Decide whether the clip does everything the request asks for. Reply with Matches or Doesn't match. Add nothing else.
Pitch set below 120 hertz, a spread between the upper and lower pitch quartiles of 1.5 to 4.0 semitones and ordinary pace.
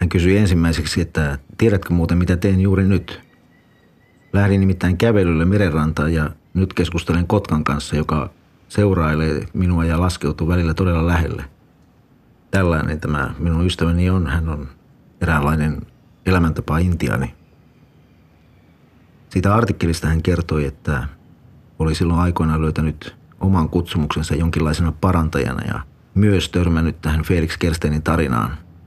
Matches